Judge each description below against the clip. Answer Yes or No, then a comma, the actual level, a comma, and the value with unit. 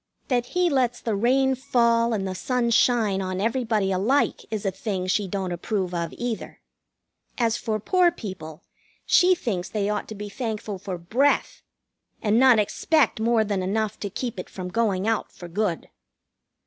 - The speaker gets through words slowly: No, average, 170 wpm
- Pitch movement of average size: Yes, average, 4.0 semitones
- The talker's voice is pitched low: No, high, 215 Hz